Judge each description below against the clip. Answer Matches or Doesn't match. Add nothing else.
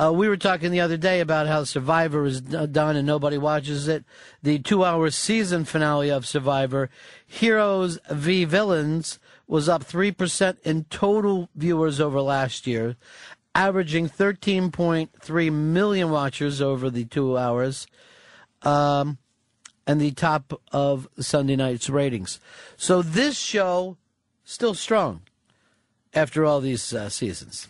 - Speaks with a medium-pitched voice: Matches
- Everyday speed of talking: Doesn't match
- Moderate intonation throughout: Matches